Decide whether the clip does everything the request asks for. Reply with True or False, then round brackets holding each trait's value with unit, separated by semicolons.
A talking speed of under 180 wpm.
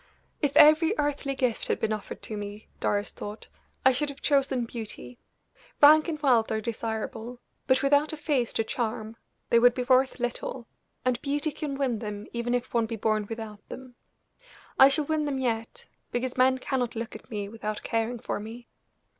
False (185 wpm)